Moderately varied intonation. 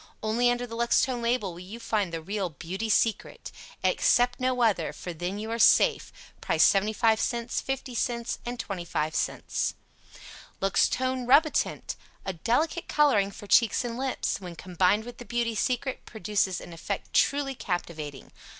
Yes: average, 4.4 semitones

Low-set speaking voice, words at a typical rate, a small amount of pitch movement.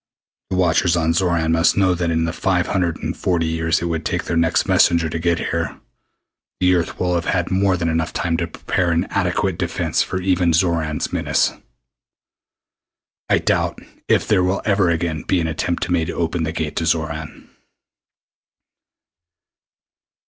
Yes: very low, 85 Hz; average, 170 wpm; narrow, 1.7 semitones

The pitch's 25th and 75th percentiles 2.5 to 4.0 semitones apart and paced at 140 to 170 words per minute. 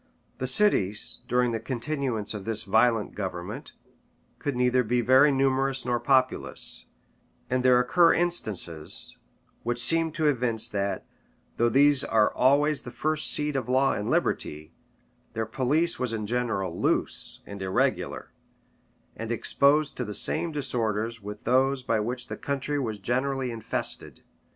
Yes: average, 3.7 semitones; average, 145 wpm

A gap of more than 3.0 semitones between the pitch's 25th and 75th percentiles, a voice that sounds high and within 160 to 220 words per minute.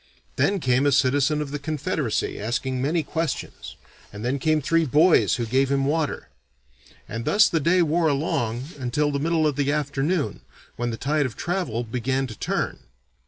No: average, 3.6 semitones; medium, 140 Hz; average, 175 wpm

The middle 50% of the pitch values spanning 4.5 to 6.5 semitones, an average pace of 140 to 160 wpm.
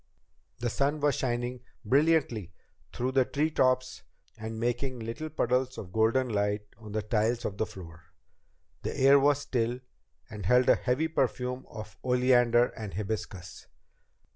No: average, 3.2 semitones; average, 145 wpm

